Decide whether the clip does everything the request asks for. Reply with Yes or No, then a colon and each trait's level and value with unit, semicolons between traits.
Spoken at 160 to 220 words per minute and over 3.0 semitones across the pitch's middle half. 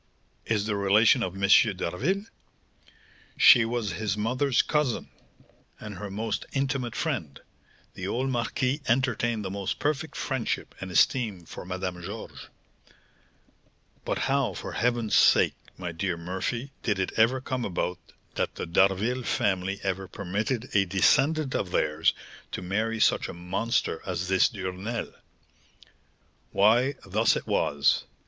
No: slow, 135 wpm; average, 4.6 semitones